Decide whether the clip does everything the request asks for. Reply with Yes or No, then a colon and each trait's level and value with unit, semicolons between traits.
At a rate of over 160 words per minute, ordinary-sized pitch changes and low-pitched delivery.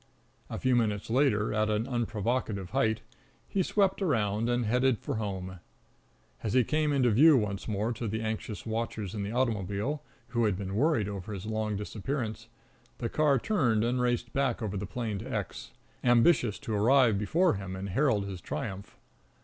Yes: average, 175 wpm; average, 3.5 semitones; low, 110 Hz